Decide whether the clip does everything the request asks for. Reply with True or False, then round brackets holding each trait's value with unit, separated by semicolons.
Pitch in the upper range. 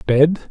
False (150 Hz)